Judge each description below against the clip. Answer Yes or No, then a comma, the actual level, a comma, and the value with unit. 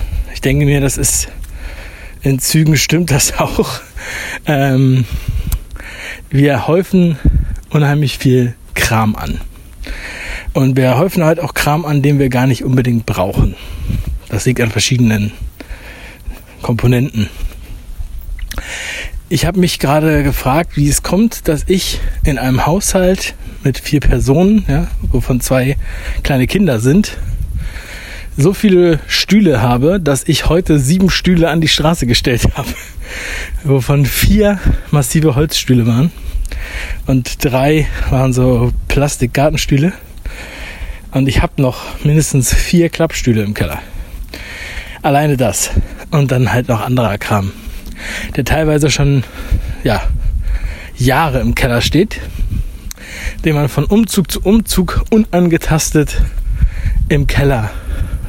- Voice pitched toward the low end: Yes, low, 130 Hz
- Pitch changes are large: Yes, wide, 7.5 semitones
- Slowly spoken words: Yes, slow, 115 wpm